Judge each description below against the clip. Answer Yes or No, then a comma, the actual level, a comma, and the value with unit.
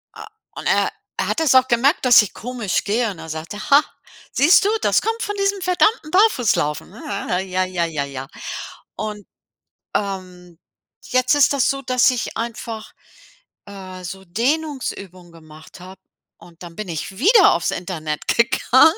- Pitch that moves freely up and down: Yes, wide, 7.4 semitones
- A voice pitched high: Yes, high, 215 Hz